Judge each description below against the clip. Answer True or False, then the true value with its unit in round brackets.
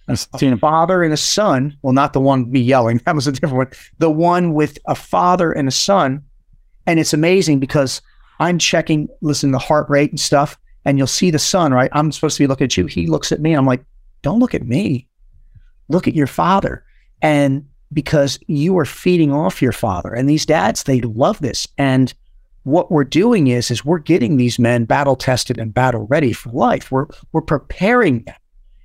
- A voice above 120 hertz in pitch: True (140 Hz)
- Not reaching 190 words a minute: False (205 wpm)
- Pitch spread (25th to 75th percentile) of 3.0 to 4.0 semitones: True (3.5 semitones)